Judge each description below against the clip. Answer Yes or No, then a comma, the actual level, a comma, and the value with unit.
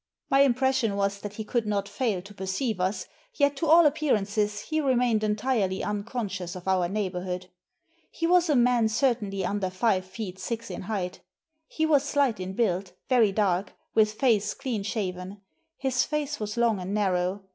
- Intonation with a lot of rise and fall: No, average, 4.6 semitones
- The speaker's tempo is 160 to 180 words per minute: Yes, average, 170 wpm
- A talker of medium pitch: No, high, 210 Hz